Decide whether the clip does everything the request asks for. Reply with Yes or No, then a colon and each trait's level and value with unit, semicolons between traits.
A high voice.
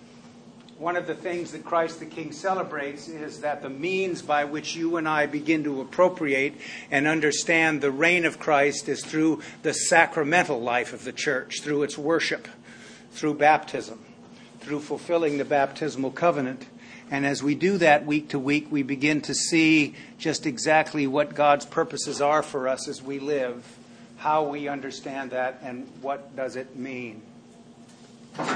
No: medium, 150 Hz